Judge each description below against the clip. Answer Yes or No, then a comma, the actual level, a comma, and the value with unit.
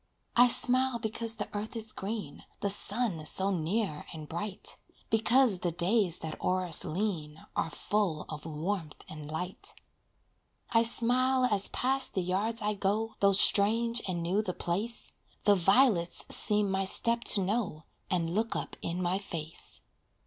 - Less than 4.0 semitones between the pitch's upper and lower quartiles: No, average, 4.6 semitones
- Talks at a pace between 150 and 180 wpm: Yes, average, 155 wpm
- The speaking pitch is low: No, high, 200 Hz